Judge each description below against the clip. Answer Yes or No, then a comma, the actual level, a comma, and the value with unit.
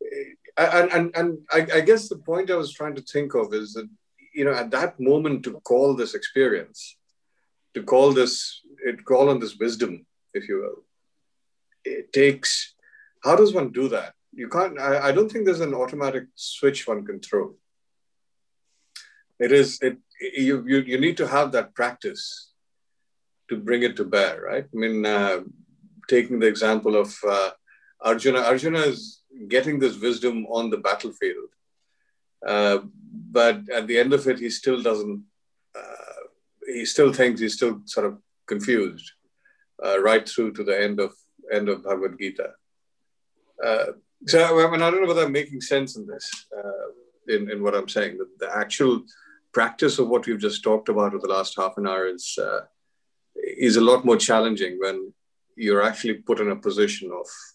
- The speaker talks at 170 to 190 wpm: Yes, average, 175 wpm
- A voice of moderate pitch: Yes, medium, 145 Hz